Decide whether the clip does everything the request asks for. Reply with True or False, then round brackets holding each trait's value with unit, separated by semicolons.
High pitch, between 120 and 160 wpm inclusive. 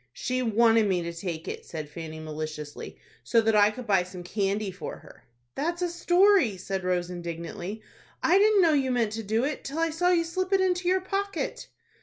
False (225 Hz; 205 wpm)